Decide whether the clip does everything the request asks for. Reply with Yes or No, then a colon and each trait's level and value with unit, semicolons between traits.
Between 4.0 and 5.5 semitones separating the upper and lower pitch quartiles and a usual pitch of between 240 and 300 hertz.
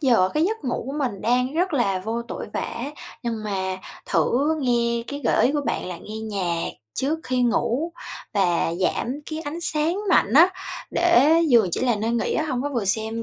Yes: average, 5.1 semitones; high, 245 Hz